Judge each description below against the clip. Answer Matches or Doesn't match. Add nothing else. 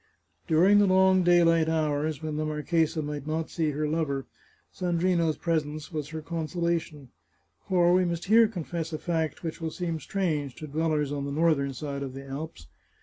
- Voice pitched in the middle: Matches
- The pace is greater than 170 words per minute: Matches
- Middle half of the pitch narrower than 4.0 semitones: Matches